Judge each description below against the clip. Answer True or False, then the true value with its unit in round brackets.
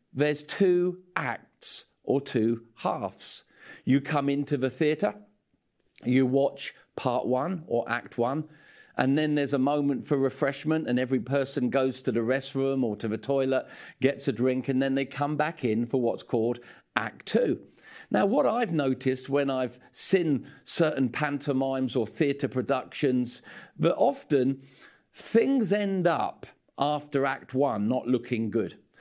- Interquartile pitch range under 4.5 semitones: True (2.5 semitones)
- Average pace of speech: True (150 wpm)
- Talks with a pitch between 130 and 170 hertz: True (135 Hz)